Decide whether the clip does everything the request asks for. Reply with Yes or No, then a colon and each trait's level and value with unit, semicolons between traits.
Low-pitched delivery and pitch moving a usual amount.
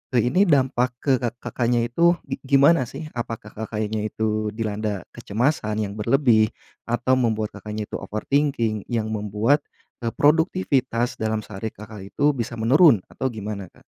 Yes: low, 115 Hz; average, 3.6 semitones